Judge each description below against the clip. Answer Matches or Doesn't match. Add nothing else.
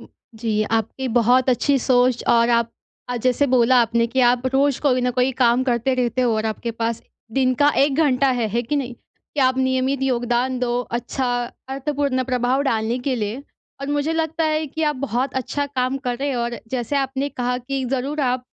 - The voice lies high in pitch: Matches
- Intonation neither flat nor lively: Doesn't match